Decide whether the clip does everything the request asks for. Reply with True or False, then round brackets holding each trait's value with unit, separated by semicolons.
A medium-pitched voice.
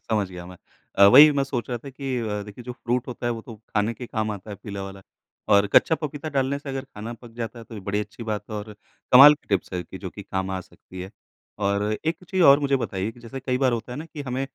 False (115 Hz)